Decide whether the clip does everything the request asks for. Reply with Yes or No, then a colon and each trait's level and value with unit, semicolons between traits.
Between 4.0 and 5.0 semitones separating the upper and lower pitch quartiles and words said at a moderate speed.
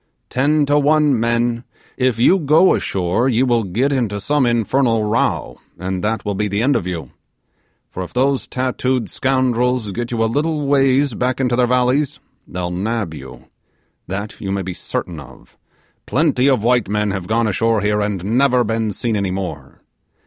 Yes: average, 4.3 semitones; average, 180 wpm